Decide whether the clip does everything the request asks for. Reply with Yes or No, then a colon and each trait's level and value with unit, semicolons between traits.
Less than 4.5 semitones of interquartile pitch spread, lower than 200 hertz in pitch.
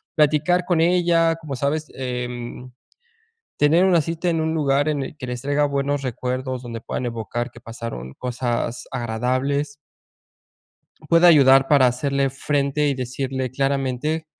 Yes: average, 3.4 semitones; medium, 140 Hz